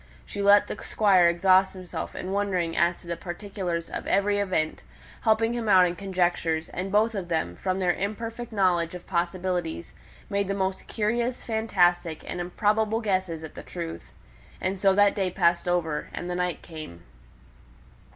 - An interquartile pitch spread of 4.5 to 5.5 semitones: No, average, 2.8 semitones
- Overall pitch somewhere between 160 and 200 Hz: Yes, medium, 185 Hz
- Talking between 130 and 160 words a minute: No, average, 170 wpm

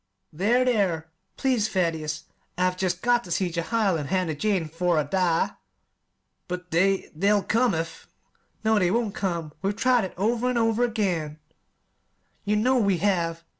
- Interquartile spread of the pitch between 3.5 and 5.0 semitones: Yes, average, 4.6 semitones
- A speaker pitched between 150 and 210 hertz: Yes, high, 190 Hz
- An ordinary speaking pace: Yes, average, 165 wpm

